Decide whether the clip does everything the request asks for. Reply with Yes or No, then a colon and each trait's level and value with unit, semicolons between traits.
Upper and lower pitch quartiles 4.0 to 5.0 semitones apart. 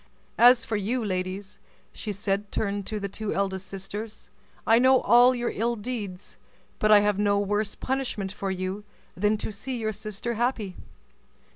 No: average, 2.8 semitones